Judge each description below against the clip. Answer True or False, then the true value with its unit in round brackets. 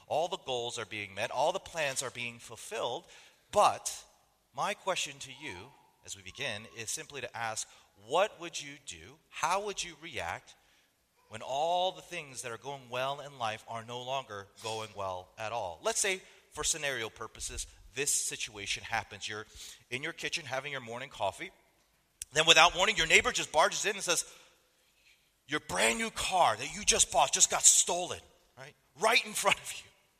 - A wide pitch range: True (7.3 semitones)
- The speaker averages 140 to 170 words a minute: False (185 wpm)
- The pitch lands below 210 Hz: True (135 Hz)